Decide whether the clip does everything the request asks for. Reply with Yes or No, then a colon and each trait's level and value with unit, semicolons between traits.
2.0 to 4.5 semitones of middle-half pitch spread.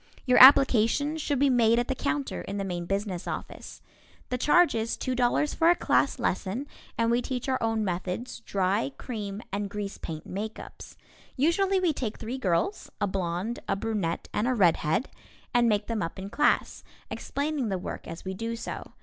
No: average, 4.9 semitones